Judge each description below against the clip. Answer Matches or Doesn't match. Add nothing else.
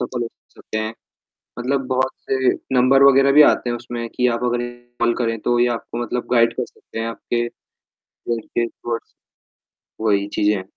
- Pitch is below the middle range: Matches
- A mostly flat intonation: Matches